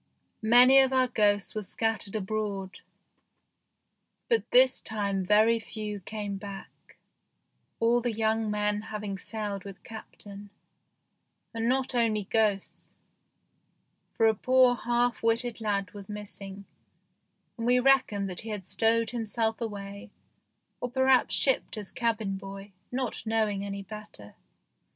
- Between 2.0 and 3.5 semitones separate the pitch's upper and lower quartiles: Yes, average, 2.7 semitones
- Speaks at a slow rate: Yes, slow, 130 wpm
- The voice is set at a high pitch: Yes, high, 215 Hz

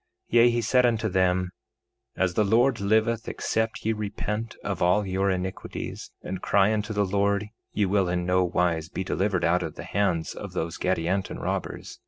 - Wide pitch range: No, average, 2.9 semitones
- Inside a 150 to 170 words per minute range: No, average, 185 wpm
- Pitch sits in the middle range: No, low, 100 Hz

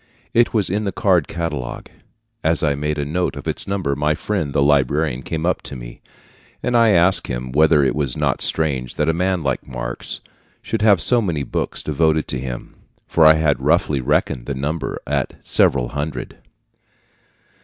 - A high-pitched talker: No, very low, 75 Hz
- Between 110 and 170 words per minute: No, average, 185 wpm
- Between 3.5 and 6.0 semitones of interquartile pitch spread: Yes, average, 4.2 semitones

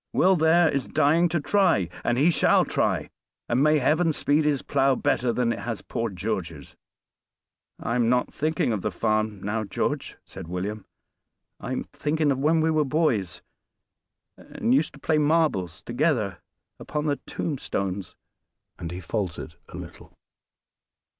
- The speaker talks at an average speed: Yes, average, 155 wpm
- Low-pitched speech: Yes, low, 130 Hz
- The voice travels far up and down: Yes, wide, 7.0 semitones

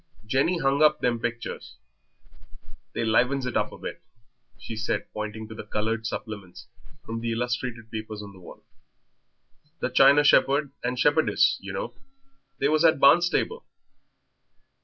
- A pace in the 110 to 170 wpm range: Yes, average, 145 wpm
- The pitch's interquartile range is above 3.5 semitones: Yes, average, 4.1 semitones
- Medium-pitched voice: No, low, 120 Hz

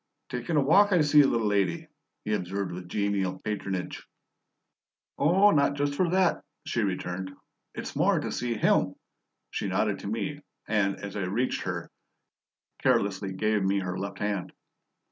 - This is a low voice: Yes, low, 105 Hz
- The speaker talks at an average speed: Yes, average, 155 wpm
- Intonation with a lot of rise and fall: Yes, wide, 6.6 semitones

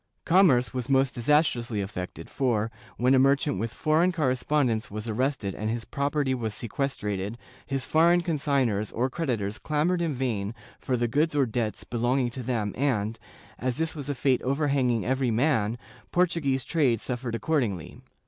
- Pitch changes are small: No, average, 4.1 semitones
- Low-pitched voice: Yes, low, 130 Hz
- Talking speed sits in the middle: Yes, average, 170 wpm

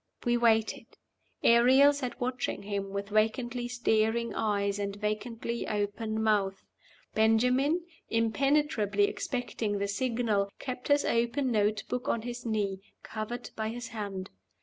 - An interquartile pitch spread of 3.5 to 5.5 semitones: No, average, 3.0 semitones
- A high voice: Yes, high, 225 Hz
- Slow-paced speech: Yes, slow, 130 wpm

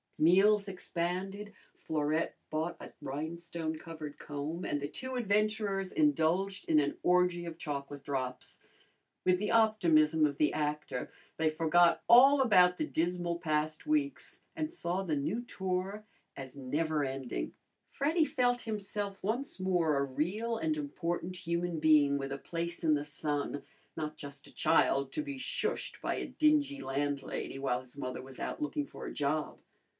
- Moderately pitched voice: Yes, medium, 170 Hz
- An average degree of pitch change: No, wide, 5.8 semitones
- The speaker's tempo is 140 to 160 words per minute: Yes, average, 155 wpm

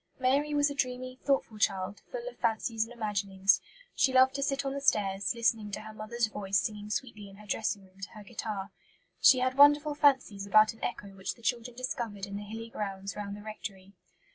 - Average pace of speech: No, fast, 210 wpm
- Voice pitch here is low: No, high, 220 Hz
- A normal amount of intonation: Yes, average, 4.2 semitones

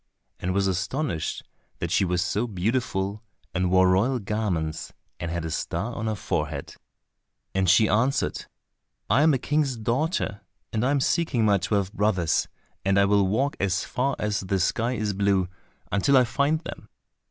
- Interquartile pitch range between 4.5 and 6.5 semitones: Yes, average, 4.8 semitones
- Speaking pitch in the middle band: No, low, 105 Hz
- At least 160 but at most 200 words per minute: Yes, average, 165 wpm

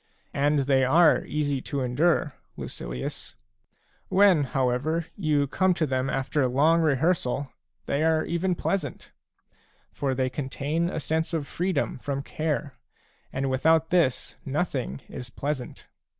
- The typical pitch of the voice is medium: Yes, medium, 145 Hz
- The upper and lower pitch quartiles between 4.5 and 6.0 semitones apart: No, average, 3.5 semitones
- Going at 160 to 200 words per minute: No, slow, 135 wpm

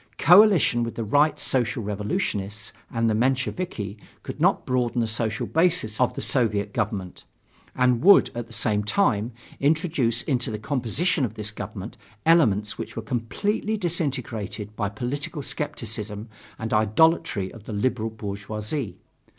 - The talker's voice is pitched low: Yes, low, 115 Hz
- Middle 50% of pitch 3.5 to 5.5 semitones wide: Yes, average, 4.9 semitones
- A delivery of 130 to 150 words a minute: Yes, average, 140 wpm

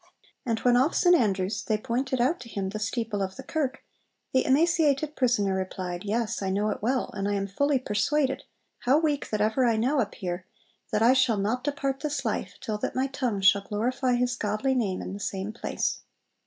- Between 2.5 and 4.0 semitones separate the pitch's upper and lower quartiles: No, average, 4.6 semitones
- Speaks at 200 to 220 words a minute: Yes, fast, 205 wpm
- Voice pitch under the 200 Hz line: No, high, 235 Hz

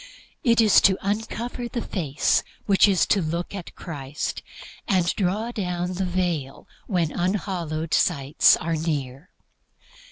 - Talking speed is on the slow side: Yes, slow, 130 wpm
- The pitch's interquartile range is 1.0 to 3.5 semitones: No, average, 4.1 semitones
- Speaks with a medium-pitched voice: Yes, medium, 180 Hz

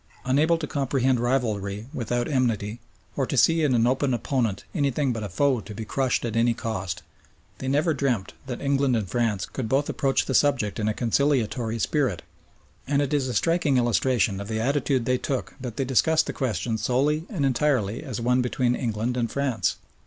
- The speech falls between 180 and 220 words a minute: Yes, average, 190 wpm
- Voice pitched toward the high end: No, low, 125 Hz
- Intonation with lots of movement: No, average, 3.6 semitones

